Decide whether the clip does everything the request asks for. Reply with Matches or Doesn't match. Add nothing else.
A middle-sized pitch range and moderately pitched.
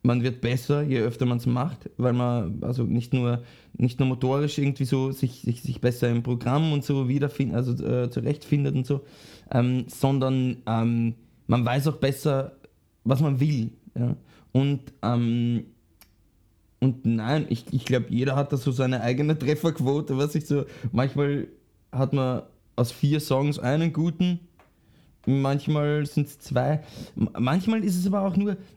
Doesn't match